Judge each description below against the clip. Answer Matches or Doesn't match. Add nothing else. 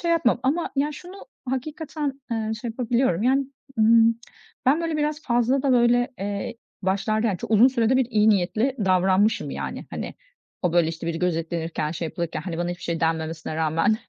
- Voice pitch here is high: Matches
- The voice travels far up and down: Matches